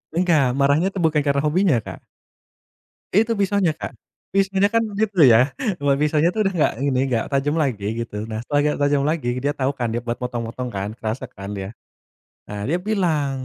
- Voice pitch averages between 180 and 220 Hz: No, medium, 145 Hz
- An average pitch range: No, wide, 6.5 semitones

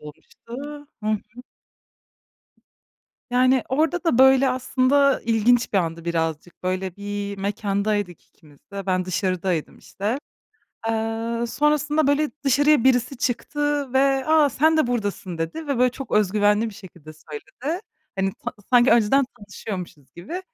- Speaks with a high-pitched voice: Yes, high, 230 Hz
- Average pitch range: No, wide, 6.0 semitones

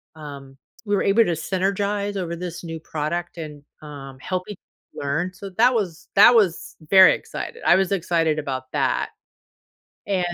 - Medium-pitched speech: Yes, medium, 175 Hz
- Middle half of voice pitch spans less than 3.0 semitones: No, average, 4.3 semitones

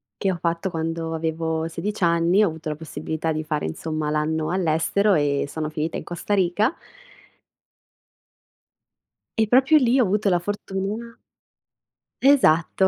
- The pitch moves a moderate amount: Yes, average, 4.1 semitones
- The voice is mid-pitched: Yes, medium, 165 Hz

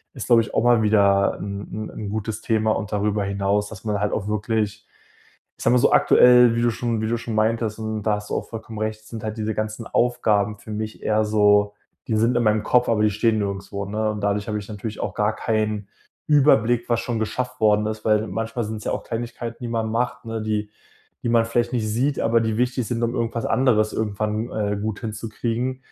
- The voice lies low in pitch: Yes, low, 110 Hz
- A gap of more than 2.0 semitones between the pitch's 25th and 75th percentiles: No, narrow, 1.7 semitones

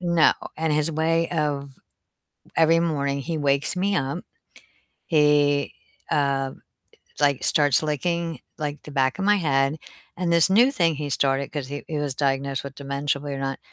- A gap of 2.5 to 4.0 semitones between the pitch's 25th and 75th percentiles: Yes, average, 2.9 semitones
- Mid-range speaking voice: Yes, medium, 145 Hz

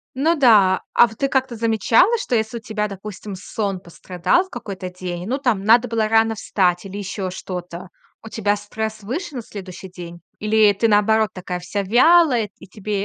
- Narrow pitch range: No, average, 3.4 semitones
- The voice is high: Yes, high, 210 Hz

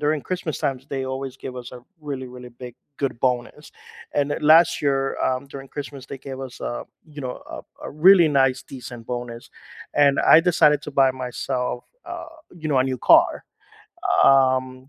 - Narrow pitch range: Yes, narrow, 2.3 semitones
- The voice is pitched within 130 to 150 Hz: Yes, low, 135 Hz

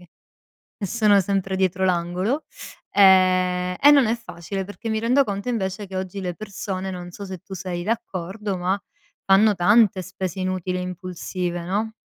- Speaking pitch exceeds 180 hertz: Yes, high, 190 Hz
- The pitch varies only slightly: Yes, narrow, 2.2 semitones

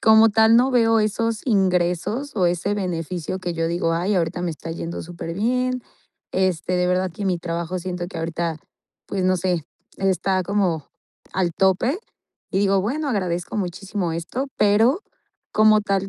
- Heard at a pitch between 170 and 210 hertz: Yes, medium, 185 Hz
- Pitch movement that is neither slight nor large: Yes, average, 3.6 semitones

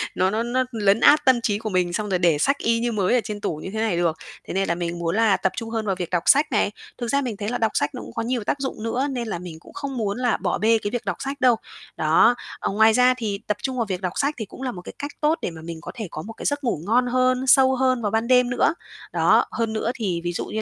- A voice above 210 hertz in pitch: Yes, high, 225 Hz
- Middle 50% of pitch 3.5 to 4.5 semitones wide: No, average, 4.9 semitones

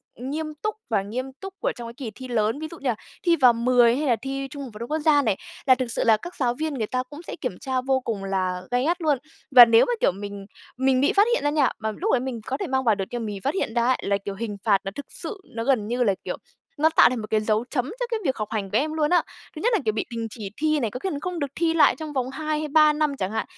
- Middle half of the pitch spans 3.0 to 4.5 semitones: No, average, 5.2 semitones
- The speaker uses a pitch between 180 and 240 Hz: No, very high, 255 Hz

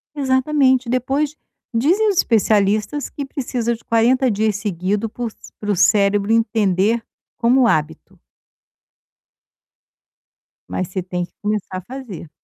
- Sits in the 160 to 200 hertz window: No, high, 225 Hz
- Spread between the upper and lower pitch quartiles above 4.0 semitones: Yes, average, 4.4 semitones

